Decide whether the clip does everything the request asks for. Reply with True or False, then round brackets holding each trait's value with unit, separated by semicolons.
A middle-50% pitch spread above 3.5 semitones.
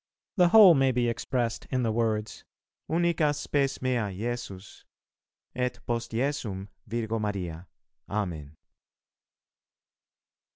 True (4.3 semitones)